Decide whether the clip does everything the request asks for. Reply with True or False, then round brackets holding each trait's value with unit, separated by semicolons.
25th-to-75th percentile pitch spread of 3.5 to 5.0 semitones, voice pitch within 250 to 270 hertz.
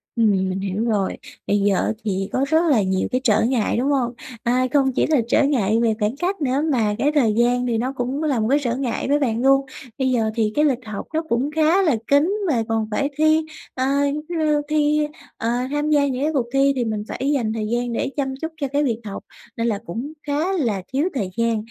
True (4.5 semitones; 255 Hz)